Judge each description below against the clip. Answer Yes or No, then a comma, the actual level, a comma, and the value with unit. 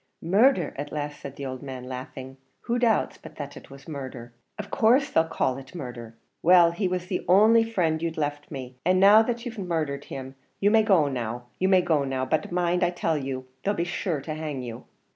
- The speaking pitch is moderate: Yes, medium, 155 Hz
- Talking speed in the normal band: No, fast, 220 wpm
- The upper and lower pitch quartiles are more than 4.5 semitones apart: Yes, wide, 5.6 semitones